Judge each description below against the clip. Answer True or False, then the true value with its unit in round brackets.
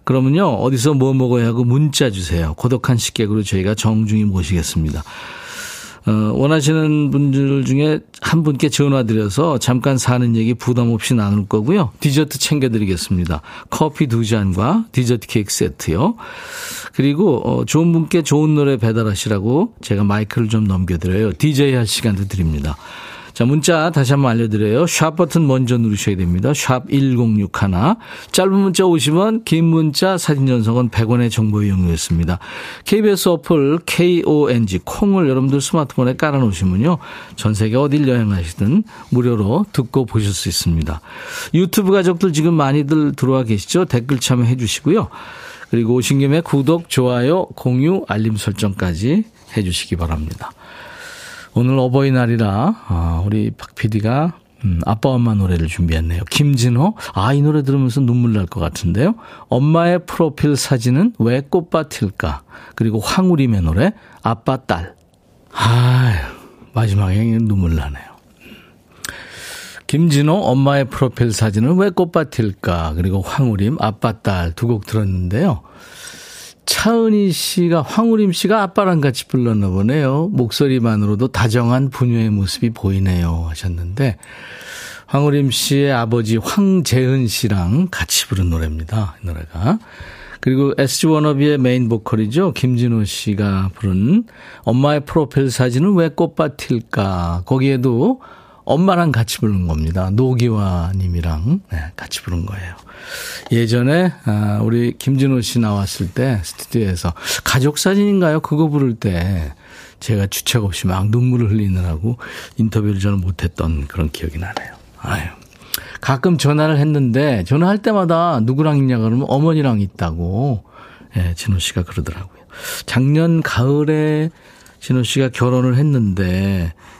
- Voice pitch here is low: True (125 Hz)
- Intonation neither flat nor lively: False (6.4 semitones)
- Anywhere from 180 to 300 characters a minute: False (310 characters per minute)